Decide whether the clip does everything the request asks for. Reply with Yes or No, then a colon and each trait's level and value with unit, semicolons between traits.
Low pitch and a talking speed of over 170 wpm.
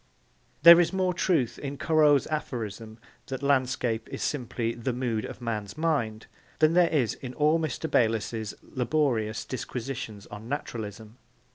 No: low, 125 Hz; average, 150 wpm